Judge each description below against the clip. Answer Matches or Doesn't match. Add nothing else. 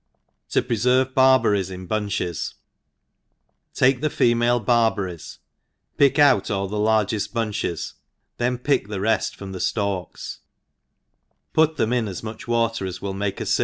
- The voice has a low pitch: Matches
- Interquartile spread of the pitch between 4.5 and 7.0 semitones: Doesn't match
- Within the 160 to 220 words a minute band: Doesn't match